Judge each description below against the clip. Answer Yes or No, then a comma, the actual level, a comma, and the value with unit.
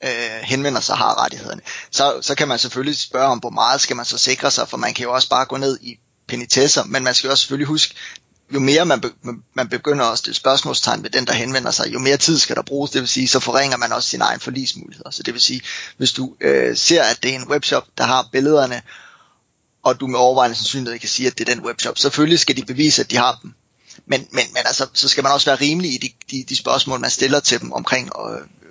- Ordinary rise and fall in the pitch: No, narrow, 1.9 semitones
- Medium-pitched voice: No, low, 130 Hz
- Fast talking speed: Yes, fast, 255 wpm